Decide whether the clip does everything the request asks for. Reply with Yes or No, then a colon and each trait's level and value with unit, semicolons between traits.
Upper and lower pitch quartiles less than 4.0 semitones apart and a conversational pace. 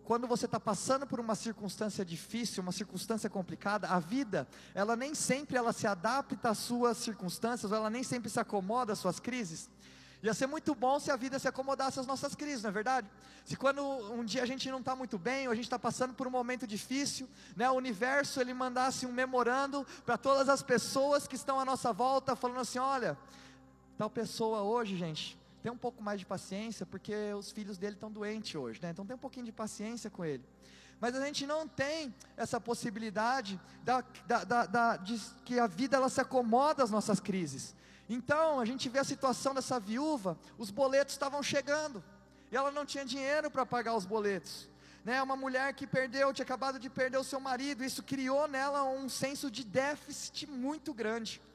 No: average, 3.6 semitones; fast, 200 wpm